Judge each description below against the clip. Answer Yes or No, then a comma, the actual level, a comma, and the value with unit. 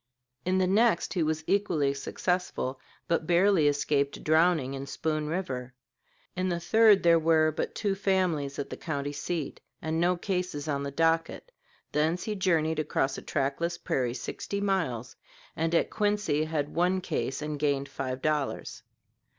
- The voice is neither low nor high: Yes, medium, 160 Hz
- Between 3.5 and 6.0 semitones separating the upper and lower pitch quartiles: Yes, average, 4.1 semitones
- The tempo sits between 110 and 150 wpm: No, average, 160 wpm